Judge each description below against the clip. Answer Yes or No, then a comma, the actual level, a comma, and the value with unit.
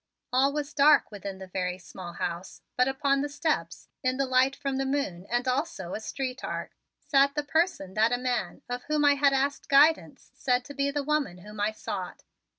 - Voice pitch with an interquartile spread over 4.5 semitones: Yes, average, 5.2 semitones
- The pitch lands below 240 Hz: No, very high, 265 Hz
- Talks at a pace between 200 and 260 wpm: Yes, fast, 205 wpm